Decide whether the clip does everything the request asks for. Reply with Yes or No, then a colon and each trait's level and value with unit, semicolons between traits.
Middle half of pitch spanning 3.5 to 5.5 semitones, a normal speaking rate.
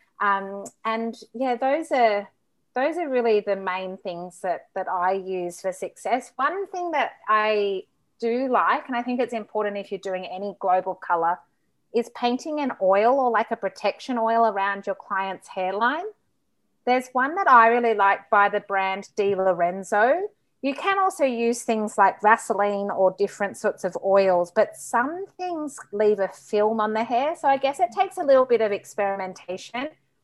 Yes: average, 4.6 semitones; average, 175 wpm